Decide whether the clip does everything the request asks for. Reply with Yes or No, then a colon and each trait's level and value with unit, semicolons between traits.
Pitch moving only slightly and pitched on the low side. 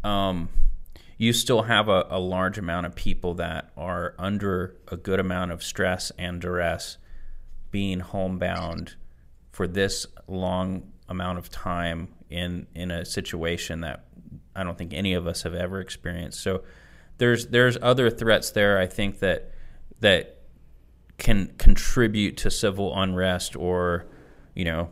Yes: narrow, 2.2 semitones; very low, 90 Hz